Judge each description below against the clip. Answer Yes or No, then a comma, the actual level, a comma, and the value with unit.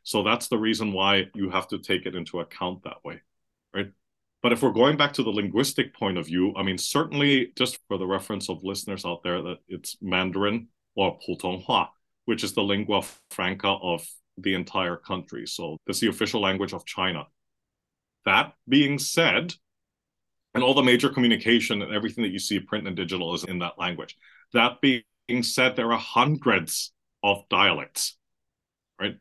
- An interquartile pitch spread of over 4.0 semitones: Yes, average, 4.6 semitones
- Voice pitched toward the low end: Yes, low, 100 Hz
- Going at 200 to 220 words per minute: No, average, 180 wpm